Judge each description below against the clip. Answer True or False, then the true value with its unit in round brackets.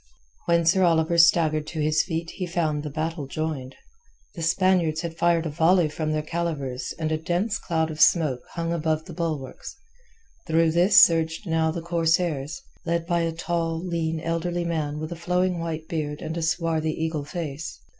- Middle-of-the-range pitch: True (165 Hz)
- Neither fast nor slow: True (180 wpm)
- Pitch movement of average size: False (1.5 semitones)